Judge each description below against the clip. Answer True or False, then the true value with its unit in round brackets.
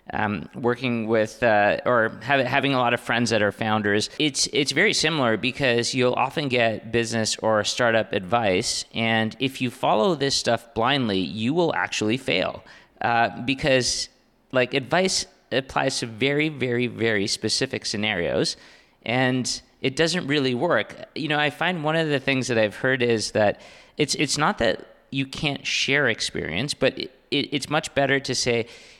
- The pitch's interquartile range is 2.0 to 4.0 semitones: True (3.4 semitones)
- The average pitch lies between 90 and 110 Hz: False (125 Hz)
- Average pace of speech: True (170 wpm)